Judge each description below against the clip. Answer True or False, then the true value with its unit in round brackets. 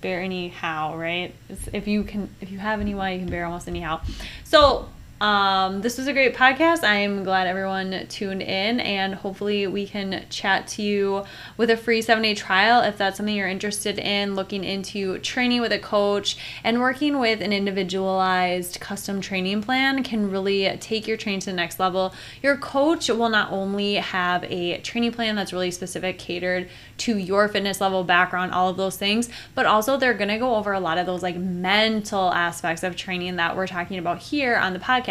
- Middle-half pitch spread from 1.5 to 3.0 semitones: True (2.6 semitones)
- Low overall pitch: False (195 Hz)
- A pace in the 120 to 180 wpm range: False (205 wpm)